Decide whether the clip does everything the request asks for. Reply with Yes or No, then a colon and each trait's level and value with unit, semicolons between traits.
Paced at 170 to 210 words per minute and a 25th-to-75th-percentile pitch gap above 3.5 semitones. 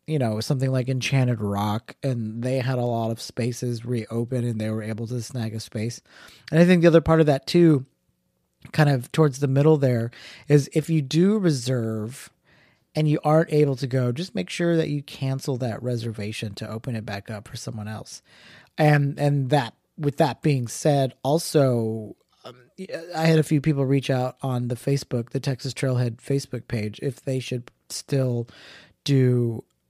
Yes: average, 185 wpm; average, 4.0 semitones